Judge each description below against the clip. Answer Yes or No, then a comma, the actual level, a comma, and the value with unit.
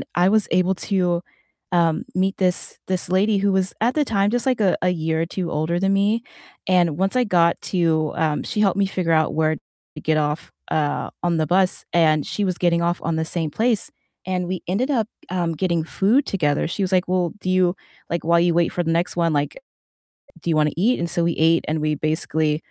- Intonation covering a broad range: No, average, 3.0 semitones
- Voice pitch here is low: No, medium, 175 Hz